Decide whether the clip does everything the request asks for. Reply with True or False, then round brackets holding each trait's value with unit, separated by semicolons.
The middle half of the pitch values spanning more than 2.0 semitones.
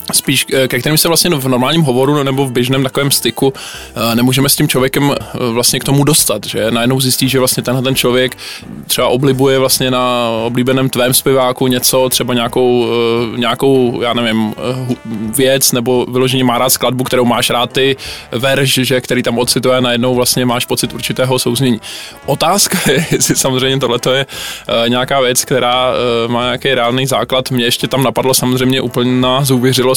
False (1.4 semitones)